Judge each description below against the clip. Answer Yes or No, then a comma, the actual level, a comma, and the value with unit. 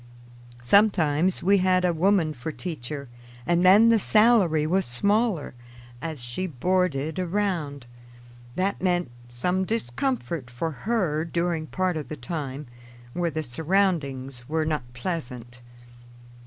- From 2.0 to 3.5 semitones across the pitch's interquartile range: No, average, 4.7 semitones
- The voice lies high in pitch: No, medium, 165 Hz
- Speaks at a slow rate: Yes, slow, 125 wpm